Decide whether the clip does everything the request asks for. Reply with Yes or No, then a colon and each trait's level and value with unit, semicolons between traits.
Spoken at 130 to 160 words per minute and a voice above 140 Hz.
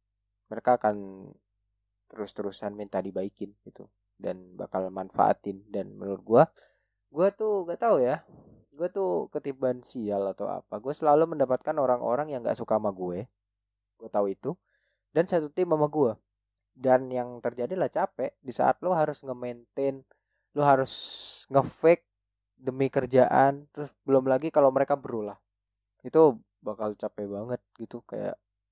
No: fast, 140 wpm; low, 115 Hz